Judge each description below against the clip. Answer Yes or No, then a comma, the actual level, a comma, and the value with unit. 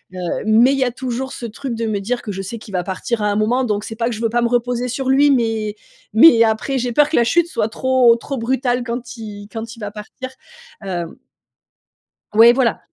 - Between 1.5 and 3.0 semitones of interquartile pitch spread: Yes, average, 2.7 semitones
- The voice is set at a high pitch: Yes, high, 235 Hz